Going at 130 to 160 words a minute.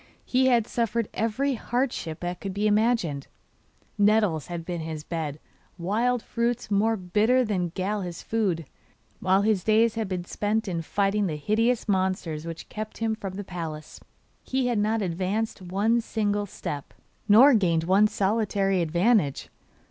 Yes: average, 155 wpm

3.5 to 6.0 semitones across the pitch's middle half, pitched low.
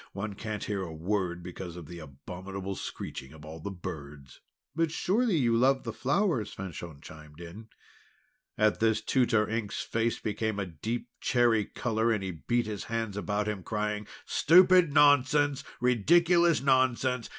Yes: wide, 5.4 semitones; low, 110 Hz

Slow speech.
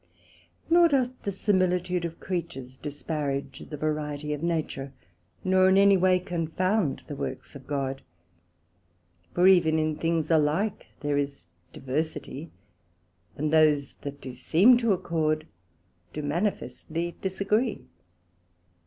Yes: slow, 120 wpm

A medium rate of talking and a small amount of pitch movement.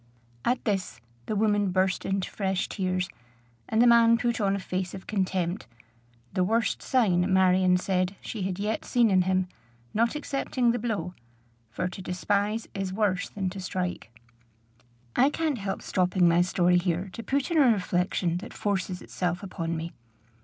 No: average, 165 wpm; average, 3.1 semitones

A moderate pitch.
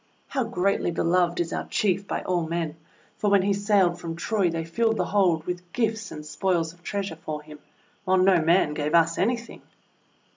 Yes: medium, 180 Hz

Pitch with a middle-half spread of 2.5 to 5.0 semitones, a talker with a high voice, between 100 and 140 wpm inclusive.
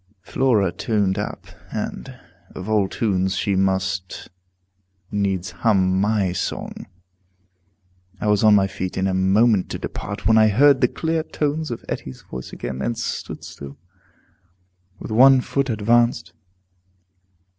No: average, 3.8 semitones; low, 100 Hz; slow, 135 wpm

